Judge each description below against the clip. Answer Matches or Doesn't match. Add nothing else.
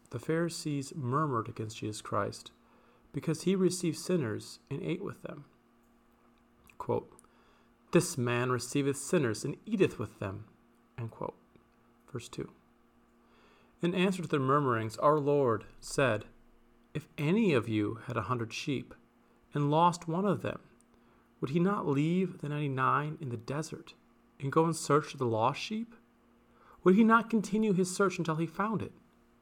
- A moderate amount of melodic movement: Doesn't match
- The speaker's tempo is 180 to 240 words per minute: Doesn't match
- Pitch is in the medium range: Matches